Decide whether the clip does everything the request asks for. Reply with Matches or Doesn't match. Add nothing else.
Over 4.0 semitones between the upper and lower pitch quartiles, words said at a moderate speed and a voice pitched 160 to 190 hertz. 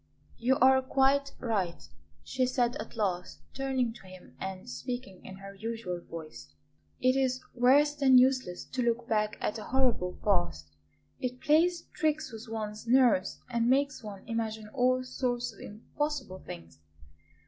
Doesn't match